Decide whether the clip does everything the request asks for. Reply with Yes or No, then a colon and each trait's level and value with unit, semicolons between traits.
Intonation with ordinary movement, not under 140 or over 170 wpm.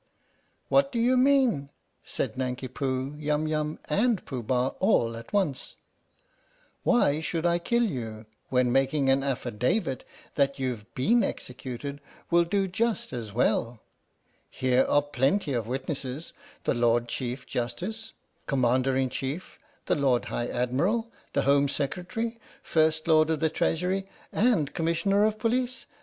No: wide, 6.8 semitones; average, 145 wpm